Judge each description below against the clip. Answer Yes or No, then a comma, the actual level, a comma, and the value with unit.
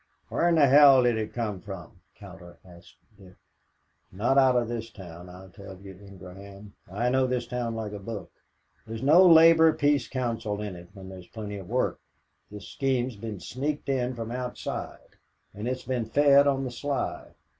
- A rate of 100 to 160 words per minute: No, average, 175 wpm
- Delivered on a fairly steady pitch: No, average, 5.0 semitones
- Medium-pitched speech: No, low, 115 Hz